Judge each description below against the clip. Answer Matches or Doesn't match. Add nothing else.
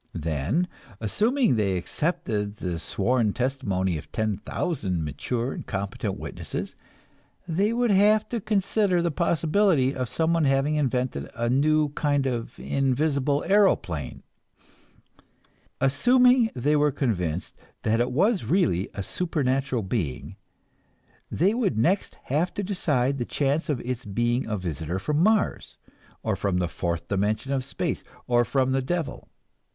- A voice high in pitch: Doesn't match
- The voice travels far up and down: Matches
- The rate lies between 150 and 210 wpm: Doesn't match